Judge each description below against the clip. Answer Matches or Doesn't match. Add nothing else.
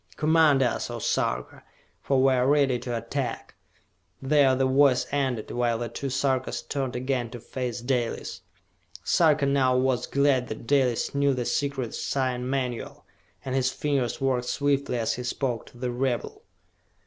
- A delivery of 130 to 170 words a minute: Matches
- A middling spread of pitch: Doesn't match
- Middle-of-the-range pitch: Doesn't match